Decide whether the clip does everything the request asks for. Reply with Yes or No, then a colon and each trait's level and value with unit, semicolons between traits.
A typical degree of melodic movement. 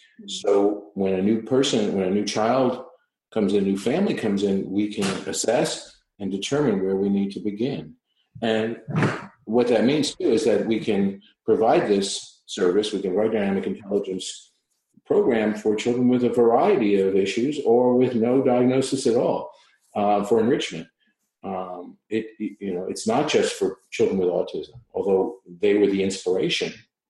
Yes: average, 4.0 semitones